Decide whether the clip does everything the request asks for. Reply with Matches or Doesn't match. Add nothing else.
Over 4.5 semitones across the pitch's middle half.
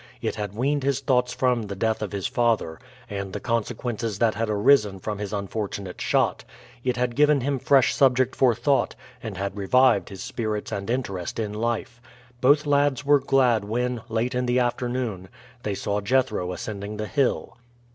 Doesn't match